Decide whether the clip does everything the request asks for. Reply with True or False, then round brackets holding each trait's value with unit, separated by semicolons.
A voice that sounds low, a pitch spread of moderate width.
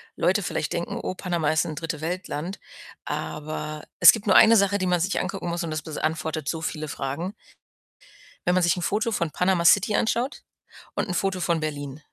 False (170 Hz; 3.5 semitones)